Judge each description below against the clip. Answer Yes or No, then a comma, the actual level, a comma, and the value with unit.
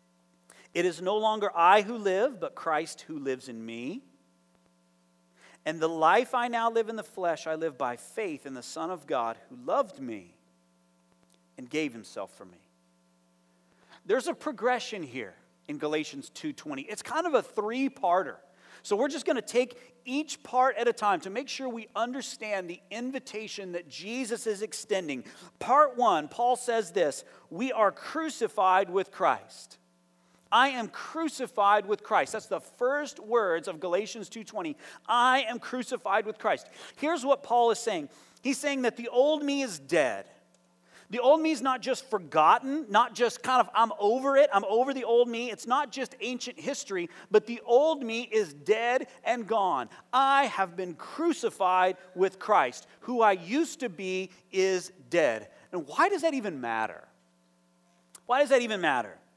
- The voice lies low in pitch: No, high, 220 Hz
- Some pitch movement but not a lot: No, wide, 7.9 semitones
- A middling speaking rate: Yes, average, 170 wpm